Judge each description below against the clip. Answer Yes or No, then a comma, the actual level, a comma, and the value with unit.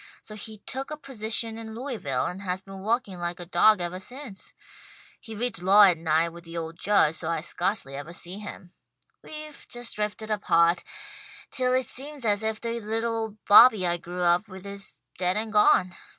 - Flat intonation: No, average, 4.2 semitones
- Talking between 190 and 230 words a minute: Yes, average, 195 wpm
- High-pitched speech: Yes, high, 205 Hz